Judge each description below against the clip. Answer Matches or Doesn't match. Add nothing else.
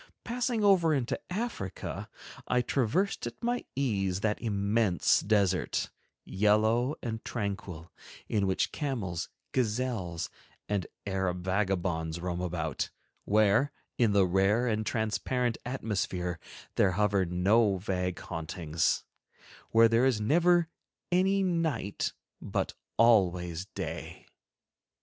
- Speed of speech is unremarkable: Doesn't match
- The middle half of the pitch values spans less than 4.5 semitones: Doesn't match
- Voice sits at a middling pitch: Doesn't match